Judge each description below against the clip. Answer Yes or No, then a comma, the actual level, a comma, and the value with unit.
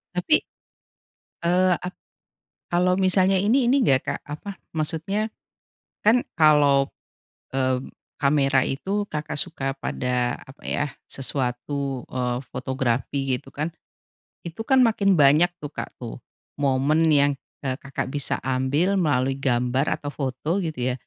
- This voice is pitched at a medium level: Yes, medium, 145 Hz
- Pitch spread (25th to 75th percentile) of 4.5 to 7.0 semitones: Yes, average, 5.3 semitones